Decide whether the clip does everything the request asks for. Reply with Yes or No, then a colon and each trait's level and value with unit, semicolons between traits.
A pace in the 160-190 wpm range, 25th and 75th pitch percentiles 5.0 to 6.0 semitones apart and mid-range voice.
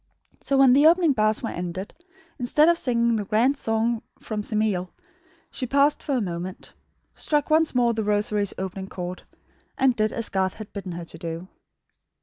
No: average, 175 wpm; wide, 5.4 semitones; high, 220 Hz